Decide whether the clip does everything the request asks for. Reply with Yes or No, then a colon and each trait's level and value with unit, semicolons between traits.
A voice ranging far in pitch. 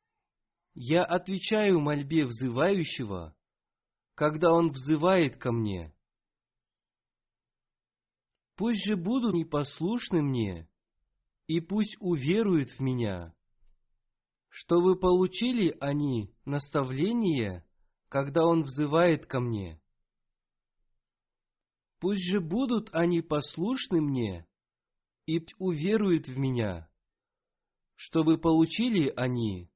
Yes: wide, 7.1 semitones